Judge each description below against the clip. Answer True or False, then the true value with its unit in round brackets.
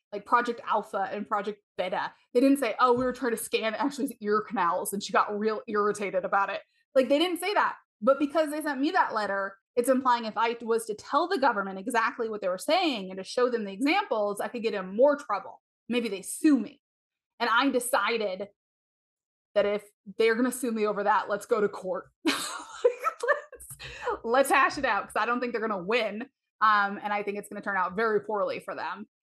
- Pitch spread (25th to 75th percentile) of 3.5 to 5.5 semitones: True (4.3 semitones)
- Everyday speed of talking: False (225 wpm)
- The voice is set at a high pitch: True (225 Hz)